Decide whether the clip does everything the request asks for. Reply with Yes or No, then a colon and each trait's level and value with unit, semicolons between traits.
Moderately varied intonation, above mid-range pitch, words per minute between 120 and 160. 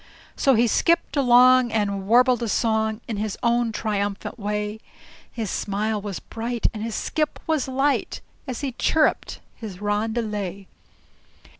Yes: average, 3.0 semitones; high, 225 Hz; average, 140 wpm